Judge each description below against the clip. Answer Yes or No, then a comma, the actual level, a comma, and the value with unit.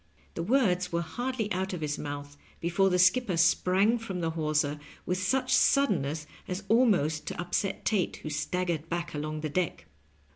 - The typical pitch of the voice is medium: Yes, medium, 180 Hz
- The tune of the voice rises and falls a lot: No, average, 4.3 semitones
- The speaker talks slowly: No, average, 170 wpm